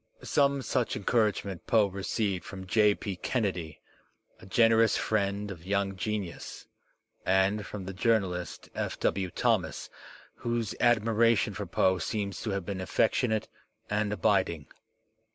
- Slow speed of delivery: Yes, slow, 130 wpm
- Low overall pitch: Yes, low, 100 Hz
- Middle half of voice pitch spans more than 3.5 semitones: No, narrow, 2.6 semitones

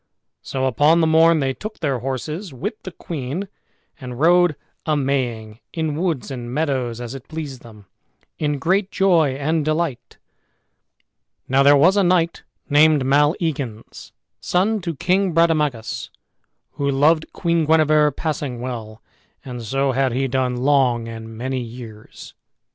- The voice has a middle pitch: Yes, medium, 145 Hz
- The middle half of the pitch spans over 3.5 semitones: Yes, average, 4.3 semitones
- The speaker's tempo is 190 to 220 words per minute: No, average, 140 wpm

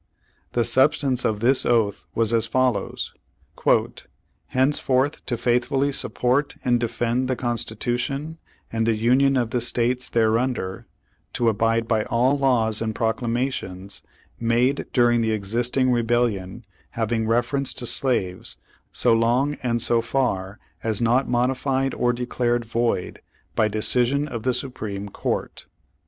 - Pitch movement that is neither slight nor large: No, narrow, 2.2 semitones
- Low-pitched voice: Yes, low, 120 Hz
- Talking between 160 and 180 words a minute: No, slow, 135 wpm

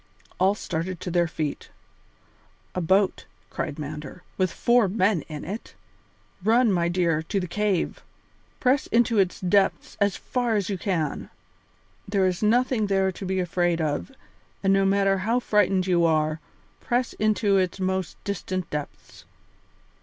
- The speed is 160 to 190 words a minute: No, average, 150 wpm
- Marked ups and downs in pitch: No, average, 3.2 semitones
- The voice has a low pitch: No, high, 190 Hz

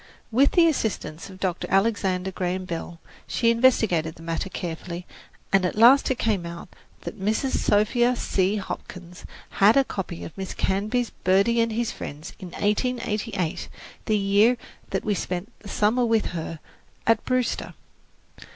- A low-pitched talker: No, high, 200 Hz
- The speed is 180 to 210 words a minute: No, average, 150 wpm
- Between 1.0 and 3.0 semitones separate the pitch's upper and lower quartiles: No, average, 4.2 semitones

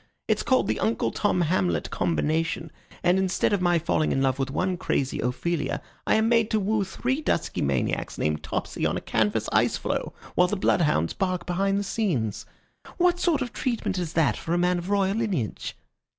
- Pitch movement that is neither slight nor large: Yes, average, 4.9 semitones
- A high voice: No, medium, 180 Hz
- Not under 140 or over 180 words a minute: No, average, 195 wpm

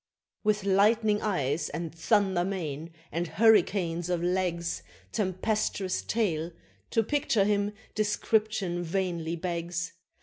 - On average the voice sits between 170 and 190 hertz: Yes, medium, 185 Hz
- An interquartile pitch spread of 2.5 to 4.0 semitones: Yes, average, 3.6 semitones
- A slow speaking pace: Yes, slow, 105 wpm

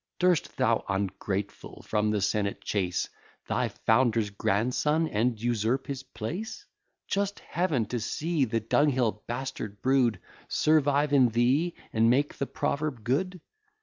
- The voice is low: Yes, low, 125 Hz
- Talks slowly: Yes, slow, 130 wpm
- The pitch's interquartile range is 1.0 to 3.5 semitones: No, average, 5.3 semitones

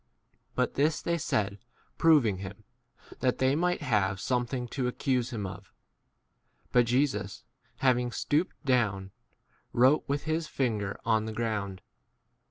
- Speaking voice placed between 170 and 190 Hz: No, low, 120 Hz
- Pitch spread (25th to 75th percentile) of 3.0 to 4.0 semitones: No, average, 5.0 semitones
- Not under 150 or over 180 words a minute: No, slow, 135 wpm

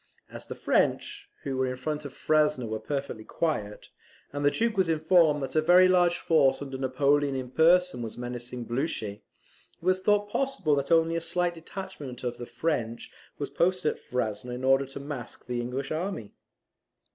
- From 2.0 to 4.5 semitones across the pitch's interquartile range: No, average, 5.1 semitones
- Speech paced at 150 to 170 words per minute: No, average, 180 wpm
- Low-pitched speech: No, medium, 145 Hz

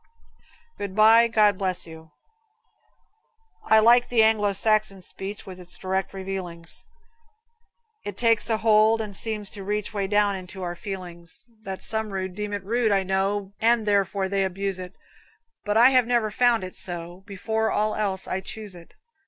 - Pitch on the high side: Yes, high, 200 Hz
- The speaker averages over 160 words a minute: Yes, average, 170 wpm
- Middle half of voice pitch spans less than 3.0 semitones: Yes, narrow, 2.4 semitones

